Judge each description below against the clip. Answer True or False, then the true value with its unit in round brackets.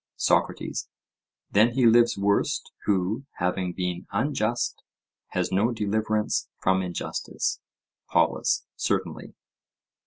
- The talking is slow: True (95 wpm)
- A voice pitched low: True (105 Hz)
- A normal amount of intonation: True (3.8 semitones)